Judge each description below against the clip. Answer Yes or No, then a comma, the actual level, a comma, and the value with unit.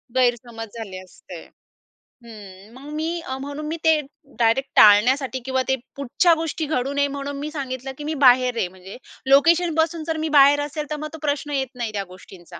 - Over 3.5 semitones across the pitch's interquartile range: Yes, average, 4.6 semitones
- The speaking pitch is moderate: No, very high, 275 Hz